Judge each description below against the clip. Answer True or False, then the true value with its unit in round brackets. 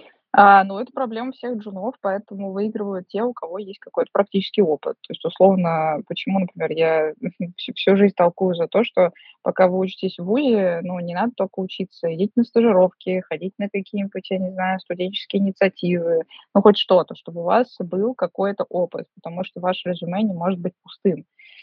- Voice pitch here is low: False (190 Hz)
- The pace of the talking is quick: True (185 wpm)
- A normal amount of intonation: False (2.1 semitones)